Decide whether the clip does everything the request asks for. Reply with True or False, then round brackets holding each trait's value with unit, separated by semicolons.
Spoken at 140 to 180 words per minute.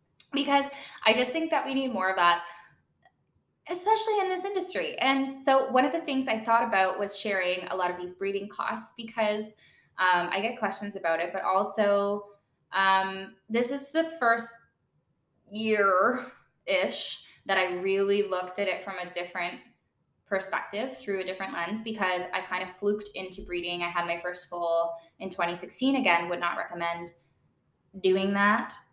True (170 wpm)